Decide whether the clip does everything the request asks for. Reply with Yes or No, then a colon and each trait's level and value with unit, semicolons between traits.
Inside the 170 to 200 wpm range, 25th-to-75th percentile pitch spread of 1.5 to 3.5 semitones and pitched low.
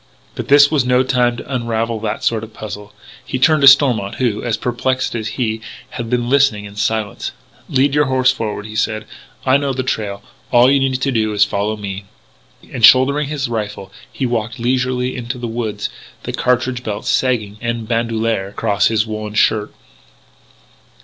Yes: average, 180 wpm; average, 3.1 semitones; low, 120 Hz